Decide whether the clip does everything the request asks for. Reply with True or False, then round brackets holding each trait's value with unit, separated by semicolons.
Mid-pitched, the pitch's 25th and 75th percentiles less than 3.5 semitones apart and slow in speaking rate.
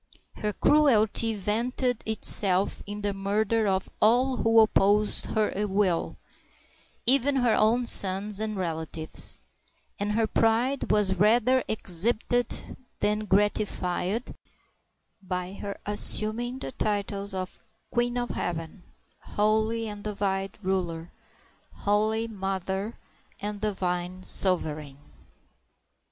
False (210 Hz; 2.9 semitones; 110 wpm)